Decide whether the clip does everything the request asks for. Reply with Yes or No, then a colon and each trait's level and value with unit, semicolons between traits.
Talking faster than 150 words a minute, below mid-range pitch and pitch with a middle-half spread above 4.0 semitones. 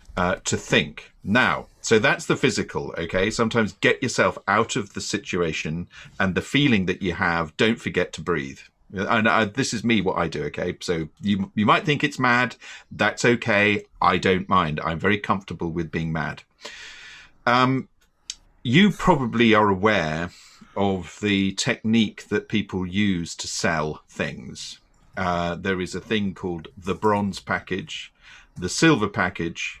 Yes: average, 160 wpm; low, 100 Hz; average, 4.5 semitones